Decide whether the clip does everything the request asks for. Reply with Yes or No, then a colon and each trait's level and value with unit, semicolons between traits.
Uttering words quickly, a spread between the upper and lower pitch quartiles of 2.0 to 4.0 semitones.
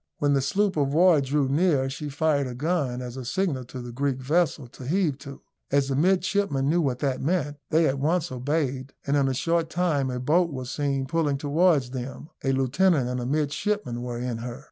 Yes: fast, 210 wpm; average, 3.7 semitones